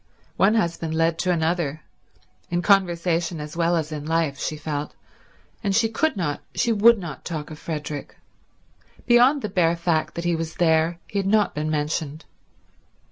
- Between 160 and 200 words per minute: Yes, average, 170 wpm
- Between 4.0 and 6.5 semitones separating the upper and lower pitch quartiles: No, average, 3.6 semitones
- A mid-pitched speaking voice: Yes, medium, 165 Hz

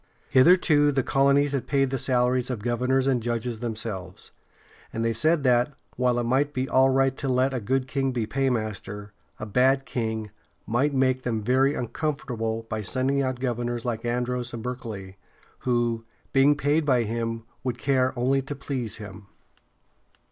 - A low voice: Yes, low, 125 Hz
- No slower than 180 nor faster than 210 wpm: No, average, 165 wpm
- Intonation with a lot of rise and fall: No, average, 2.8 semitones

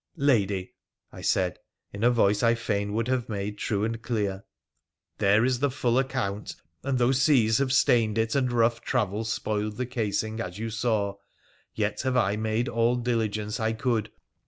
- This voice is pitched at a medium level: No, low, 110 Hz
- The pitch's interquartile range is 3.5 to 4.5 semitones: No, average, 2.9 semitones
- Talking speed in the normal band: Yes, average, 180 wpm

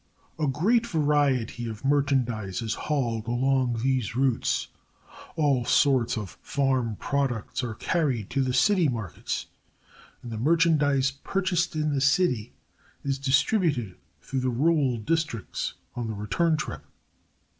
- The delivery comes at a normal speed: No, slow, 130 wpm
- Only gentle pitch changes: No, average, 4.2 semitones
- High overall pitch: No, low, 135 Hz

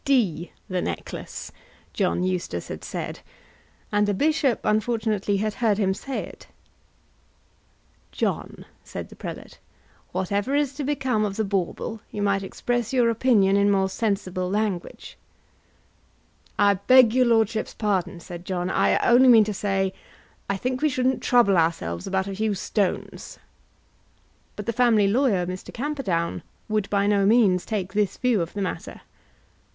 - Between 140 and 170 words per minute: Yes, average, 150 wpm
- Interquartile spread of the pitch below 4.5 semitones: Yes, average, 3.8 semitones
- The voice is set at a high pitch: Yes, high, 205 Hz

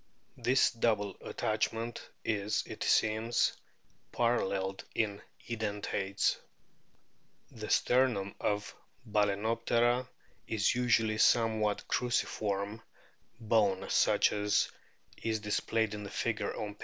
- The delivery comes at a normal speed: No, slow, 100 wpm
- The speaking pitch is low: Yes, low, 110 Hz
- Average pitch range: No, narrow, 2.1 semitones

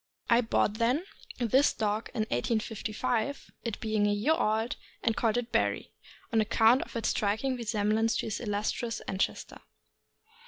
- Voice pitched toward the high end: Yes, high, 225 Hz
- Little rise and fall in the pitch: Yes, narrow, 2.0 semitones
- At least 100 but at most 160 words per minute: Yes, average, 150 wpm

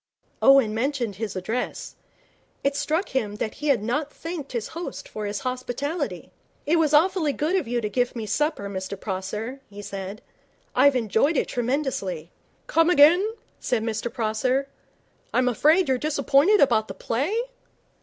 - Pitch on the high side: Yes, very high, 255 Hz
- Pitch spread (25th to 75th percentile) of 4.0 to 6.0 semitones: Yes, wide, 5.6 semitones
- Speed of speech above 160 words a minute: No, average, 155 wpm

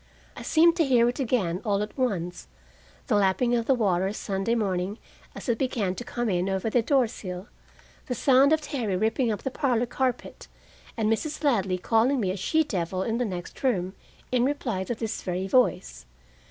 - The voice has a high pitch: Yes, high, 225 Hz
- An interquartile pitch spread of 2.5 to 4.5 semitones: No, average, 5.0 semitones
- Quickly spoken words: No, average, 190 wpm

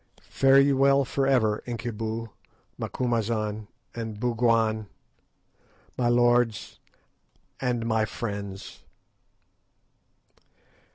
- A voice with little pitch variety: Yes, narrow, 2.1 semitones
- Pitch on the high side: No, low, 115 Hz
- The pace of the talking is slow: Yes, slow, 75 wpm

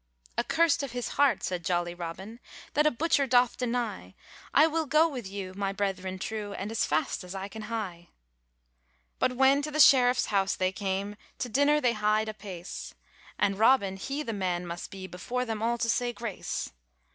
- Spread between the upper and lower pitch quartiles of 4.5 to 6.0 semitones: Yes, average, 4.8 semitones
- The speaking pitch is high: Yes, high, 215 Hz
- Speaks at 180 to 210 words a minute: Yes, average, 185 wpm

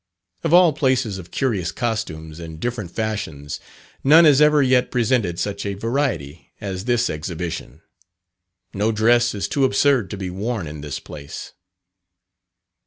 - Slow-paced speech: No, average, 145 wpm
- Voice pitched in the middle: No, low, 105 Hz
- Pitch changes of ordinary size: No, wide, 6.7 semitones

